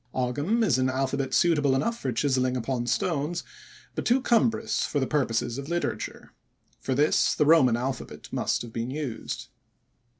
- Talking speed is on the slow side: No, average, 160 wpm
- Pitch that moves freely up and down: No, average, 3.8 semitones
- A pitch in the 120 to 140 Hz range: Yes, low, 135 Hz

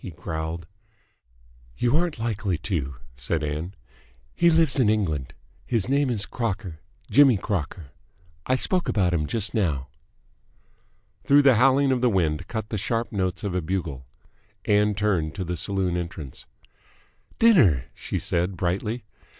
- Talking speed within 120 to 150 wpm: Yes, average, 145 wpm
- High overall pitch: No, very low, 95 Hz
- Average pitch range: No, wide, 6.1 semitones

